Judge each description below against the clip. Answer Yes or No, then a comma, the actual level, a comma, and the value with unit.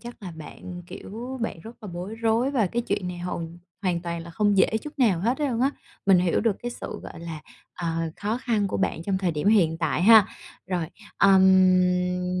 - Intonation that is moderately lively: Yes, average, 4.2 semitones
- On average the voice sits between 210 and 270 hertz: No, high, 190 Hz